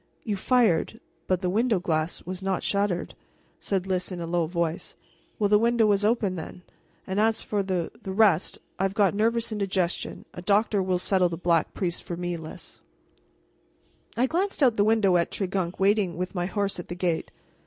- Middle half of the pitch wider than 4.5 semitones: No, average, 3.0 semitones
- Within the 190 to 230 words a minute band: Yes, average, 195 wpm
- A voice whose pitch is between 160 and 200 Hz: Yes, high, 190 Hz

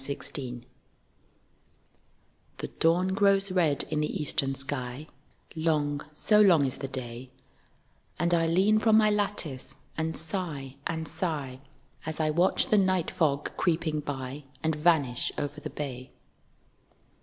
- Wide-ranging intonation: No, average, 4.4 semitones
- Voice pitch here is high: No, medium, 155 Hz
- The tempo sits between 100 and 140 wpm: Yes, slow, 135 wpm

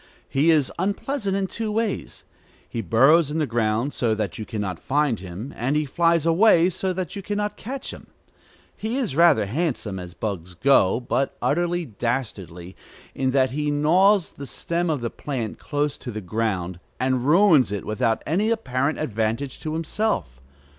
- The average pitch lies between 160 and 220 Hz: No, medium, 140 Hz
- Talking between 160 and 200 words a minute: Yes, average, 175 wpm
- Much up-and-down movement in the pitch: Yes, wide, 7.4 semitones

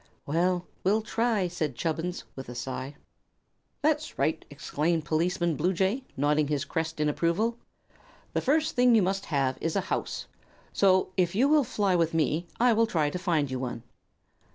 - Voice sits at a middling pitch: Yes, medium, 175 Hz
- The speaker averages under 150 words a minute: No, average, 170 wpm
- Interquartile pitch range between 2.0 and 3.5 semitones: No, average, 4.8 semitones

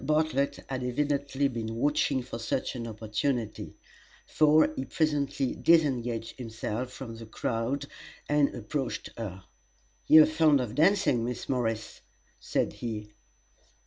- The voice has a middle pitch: No, low, 130 Hz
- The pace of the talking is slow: Yes, slow, 125 wpm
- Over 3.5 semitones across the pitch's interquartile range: Yes, average, 4.1 semitones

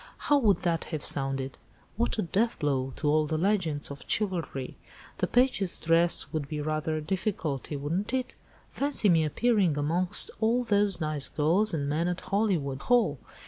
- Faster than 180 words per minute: No, average, 165 wpm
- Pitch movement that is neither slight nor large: No, wide, 5.7 semitones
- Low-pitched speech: No, medium, 165 Hz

